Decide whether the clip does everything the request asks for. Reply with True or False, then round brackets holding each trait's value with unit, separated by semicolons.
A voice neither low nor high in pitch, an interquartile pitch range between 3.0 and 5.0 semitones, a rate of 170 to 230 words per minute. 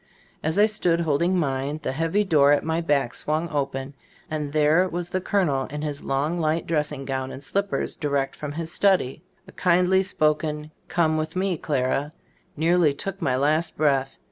True (155 Hz; 3.3 semitones; 180 wpm)